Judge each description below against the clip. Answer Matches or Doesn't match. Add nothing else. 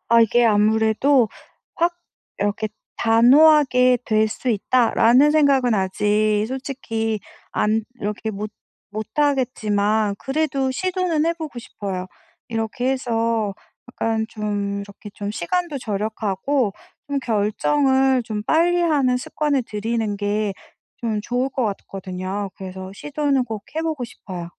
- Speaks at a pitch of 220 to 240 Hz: Matches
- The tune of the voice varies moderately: Matches